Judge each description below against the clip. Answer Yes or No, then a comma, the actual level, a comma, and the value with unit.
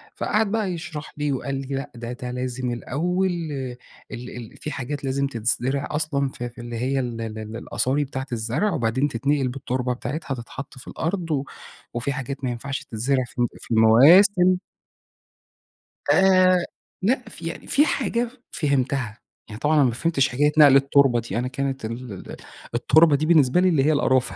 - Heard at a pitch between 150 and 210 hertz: No, low, 135 Hz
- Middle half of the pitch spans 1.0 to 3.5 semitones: No, average, 3.9 semitones